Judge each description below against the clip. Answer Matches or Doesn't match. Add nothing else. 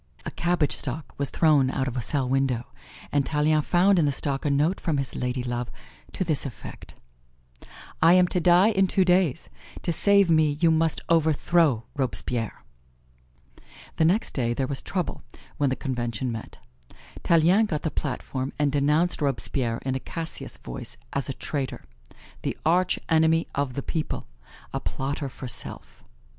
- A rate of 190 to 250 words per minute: Doesn't match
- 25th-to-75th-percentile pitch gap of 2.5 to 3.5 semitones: Doesn't match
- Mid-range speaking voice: Matches